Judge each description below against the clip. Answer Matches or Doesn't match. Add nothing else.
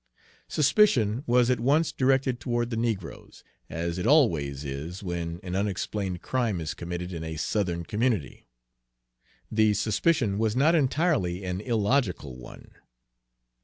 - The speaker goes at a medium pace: Doesn't match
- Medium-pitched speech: Doesn't match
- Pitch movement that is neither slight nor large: Doesn't match